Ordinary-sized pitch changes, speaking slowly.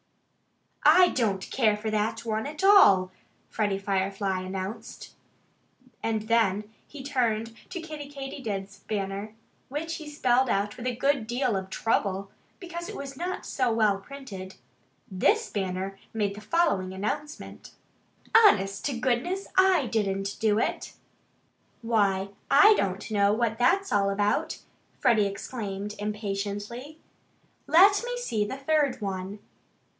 No: wide, 6.0 semitones; slow, 130 wpm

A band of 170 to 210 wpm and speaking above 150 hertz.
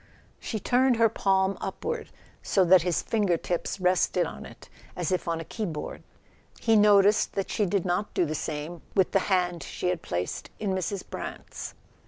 Yes: average, 180 wpm; medium, 185 Hz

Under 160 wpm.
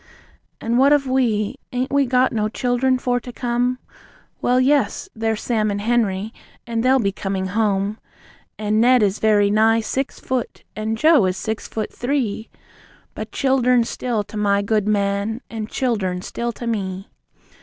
No: average, 165 wpm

